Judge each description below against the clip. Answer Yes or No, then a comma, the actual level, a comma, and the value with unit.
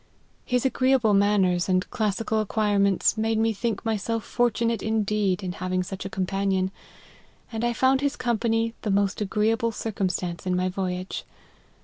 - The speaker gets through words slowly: No, average, 155 wpm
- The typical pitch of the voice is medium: No, high, 210 Hz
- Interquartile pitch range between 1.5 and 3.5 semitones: Yes, average, 3.0 semitones